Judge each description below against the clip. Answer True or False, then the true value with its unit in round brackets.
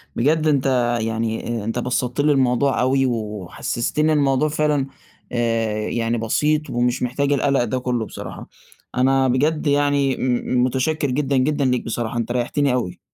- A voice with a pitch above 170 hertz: False (130 Hz)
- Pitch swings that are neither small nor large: True (3.0 semitones)